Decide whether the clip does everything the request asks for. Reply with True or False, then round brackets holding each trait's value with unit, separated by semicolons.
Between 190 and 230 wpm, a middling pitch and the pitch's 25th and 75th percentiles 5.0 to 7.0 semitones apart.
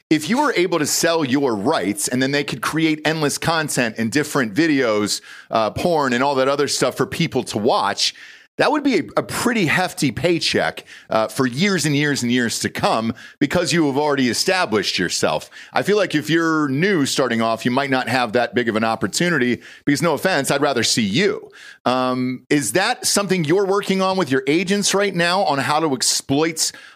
True (205 wpm; 145 Hz; 5.3 semitones)